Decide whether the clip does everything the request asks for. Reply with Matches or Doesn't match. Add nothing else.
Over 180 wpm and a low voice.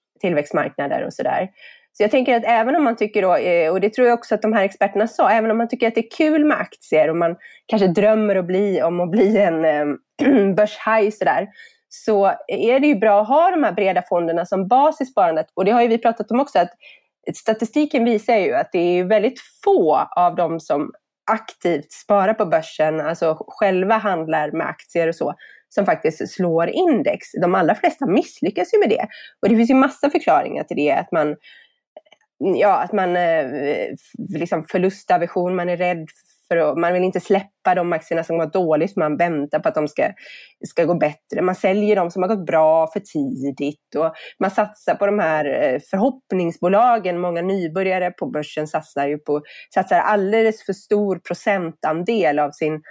Doesn't match